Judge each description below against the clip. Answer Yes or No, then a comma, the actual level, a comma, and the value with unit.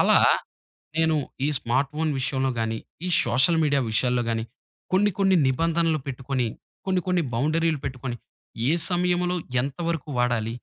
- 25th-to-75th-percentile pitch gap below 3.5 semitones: No, average, 5.2 semitones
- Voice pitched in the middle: Yes, medium, 145 Hz